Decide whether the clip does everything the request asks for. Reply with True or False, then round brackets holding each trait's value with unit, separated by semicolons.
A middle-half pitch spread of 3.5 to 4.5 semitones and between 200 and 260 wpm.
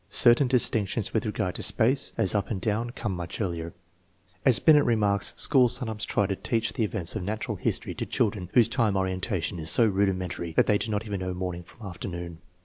True (3.8 semitones; 205 wpm)